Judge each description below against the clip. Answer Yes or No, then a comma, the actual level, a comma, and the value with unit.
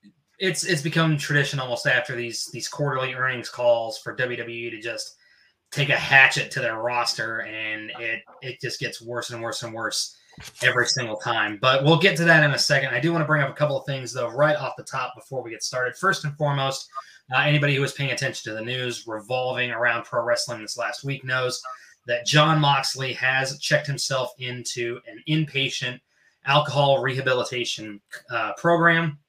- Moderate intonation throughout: Yes, average, 3.5 semitones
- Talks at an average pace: Yes, average, 195 wpm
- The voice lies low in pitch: Yes, low, 130 Hz